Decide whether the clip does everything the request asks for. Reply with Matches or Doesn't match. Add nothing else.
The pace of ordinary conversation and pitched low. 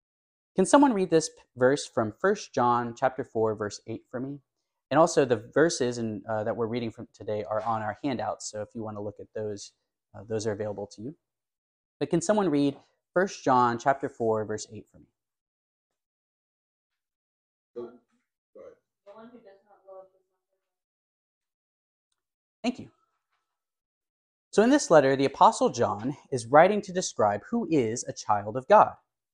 Matches